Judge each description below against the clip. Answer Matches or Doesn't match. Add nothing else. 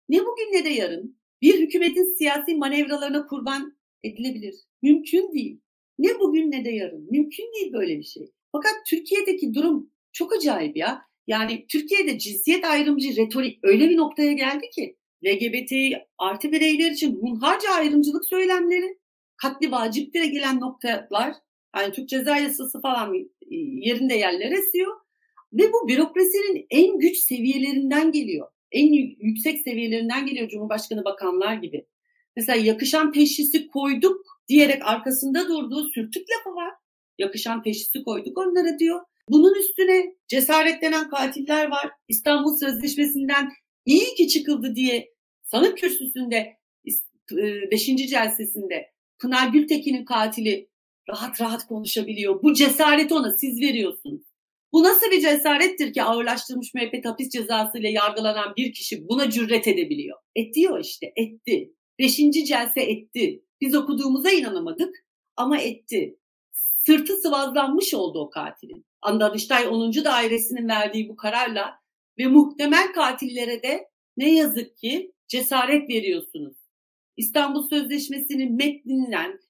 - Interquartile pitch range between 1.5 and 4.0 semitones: Doesn't match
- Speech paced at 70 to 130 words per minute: Matches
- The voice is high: Matches